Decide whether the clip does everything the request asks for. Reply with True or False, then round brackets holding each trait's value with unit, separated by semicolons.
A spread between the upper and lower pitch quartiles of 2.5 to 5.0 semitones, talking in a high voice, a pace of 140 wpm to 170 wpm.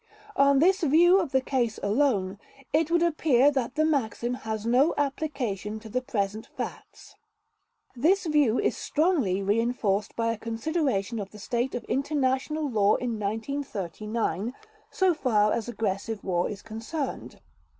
False (5.4 semitones; 240 Hz; 145 wpm)